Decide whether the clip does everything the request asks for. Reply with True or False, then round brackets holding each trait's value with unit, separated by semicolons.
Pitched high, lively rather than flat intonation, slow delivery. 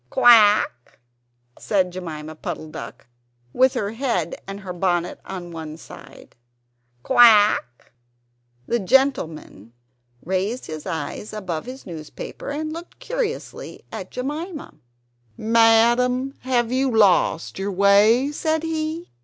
True (215 Hz; 6.7 semitones; 115 wpm)